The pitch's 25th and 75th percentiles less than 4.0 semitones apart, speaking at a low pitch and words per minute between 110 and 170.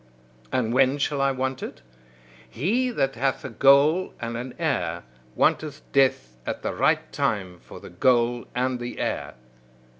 Yes: average, 2.9 semitones; low, 130 Hz; average, 155 wpm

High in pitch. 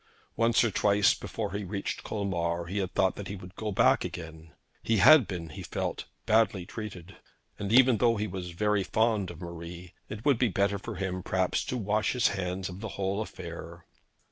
No: low, 100 Hz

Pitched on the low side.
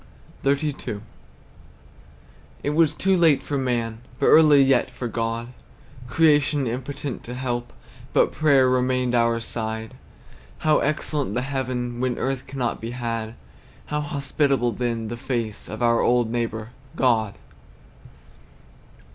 Yes: low, 125 Hz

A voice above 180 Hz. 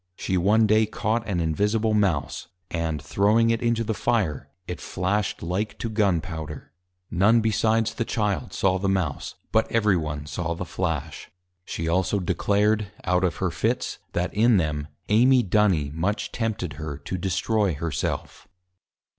No: very low, 95 Hz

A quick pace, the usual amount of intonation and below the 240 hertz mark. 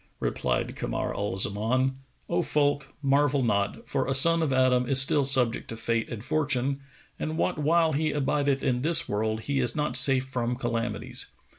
No: average, 175 wpm; average, 3.4 semitones; low, 135 Hz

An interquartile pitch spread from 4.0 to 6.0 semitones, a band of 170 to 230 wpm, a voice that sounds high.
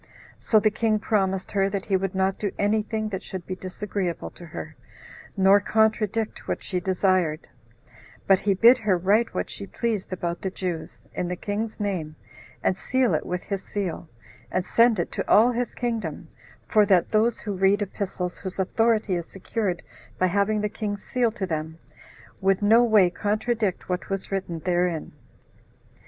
No: average, 2.8 semitones; average, 175 wpm; high, 195 Hz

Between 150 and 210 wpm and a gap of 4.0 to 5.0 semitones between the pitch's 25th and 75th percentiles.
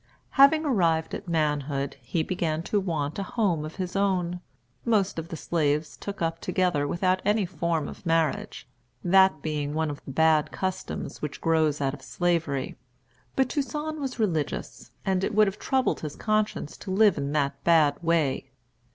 Yes: average, 170 wpm; average, 4.4 semitones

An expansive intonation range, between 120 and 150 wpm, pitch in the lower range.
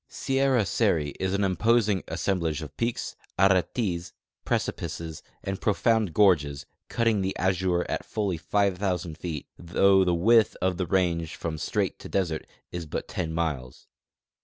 No: average, 3.2 semitones; average, 140 wpm; very low, 90 Hz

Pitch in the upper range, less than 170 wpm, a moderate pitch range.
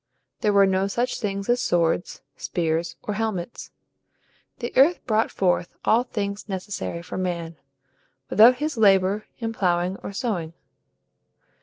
Yes: high, 200 Hz; slow, 135 wpm; average, 4.0 semitones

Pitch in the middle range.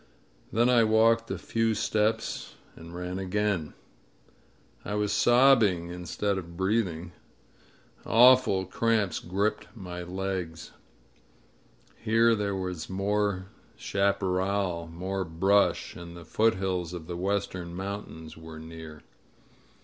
No: very low, 95 Hz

